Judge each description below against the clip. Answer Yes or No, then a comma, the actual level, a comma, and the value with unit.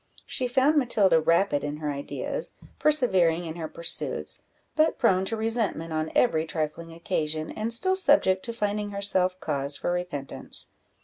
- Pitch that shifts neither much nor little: No, wide, 6.5 semitones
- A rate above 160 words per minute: No, average, 150 wpm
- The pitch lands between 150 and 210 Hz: Yes, medium, 185 Hz